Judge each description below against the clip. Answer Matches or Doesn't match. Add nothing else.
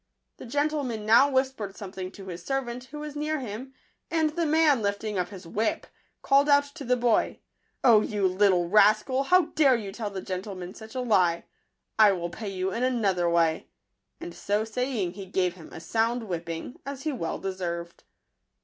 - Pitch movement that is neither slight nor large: Doesn't match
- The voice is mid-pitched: Doesn't match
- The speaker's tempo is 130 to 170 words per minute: Doesn't match